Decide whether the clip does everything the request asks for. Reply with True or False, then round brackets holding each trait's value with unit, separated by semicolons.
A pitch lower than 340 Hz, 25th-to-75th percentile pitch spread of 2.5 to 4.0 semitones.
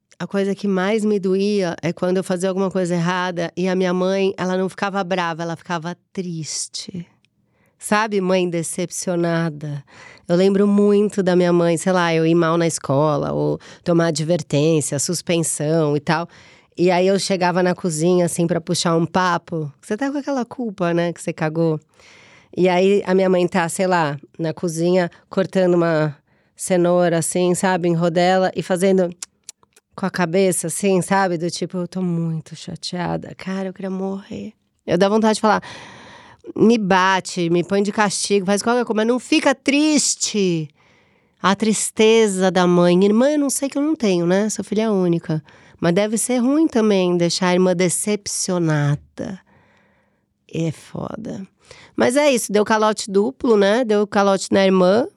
True (185 Hz; 2.9 semitones)